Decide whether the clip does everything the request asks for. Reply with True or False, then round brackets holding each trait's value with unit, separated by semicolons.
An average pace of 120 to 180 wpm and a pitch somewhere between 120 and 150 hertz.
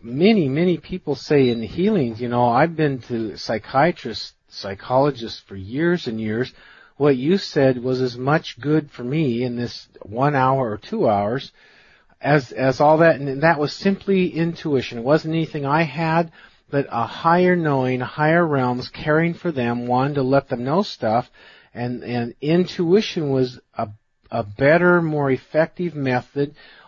True (165 wpm; 140 Hz)